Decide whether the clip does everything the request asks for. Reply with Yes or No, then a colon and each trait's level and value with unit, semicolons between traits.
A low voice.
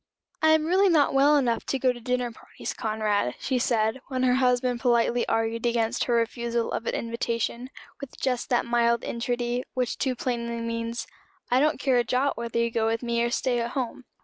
No: high, 240 Hz